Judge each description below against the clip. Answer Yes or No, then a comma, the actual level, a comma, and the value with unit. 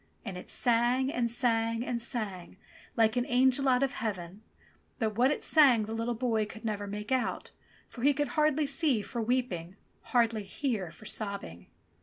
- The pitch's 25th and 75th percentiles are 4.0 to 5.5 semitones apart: No, average, 3.3 semitones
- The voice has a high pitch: Yes, high, 230 Hz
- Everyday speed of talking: Yes, average, 175 wpm